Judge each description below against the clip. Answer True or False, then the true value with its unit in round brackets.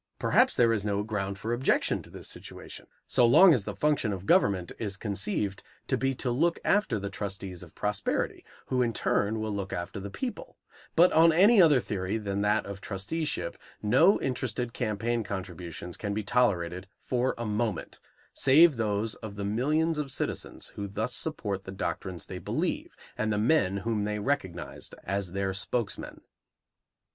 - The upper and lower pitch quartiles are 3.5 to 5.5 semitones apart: True (4.2 semitones)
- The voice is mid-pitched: False (105 Hz)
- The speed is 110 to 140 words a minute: False (170 wpm)